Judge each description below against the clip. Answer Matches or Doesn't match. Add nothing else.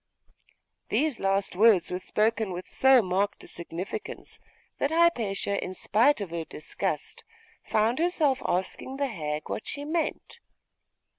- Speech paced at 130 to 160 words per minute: Matches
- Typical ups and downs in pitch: Doesn't match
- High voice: Matches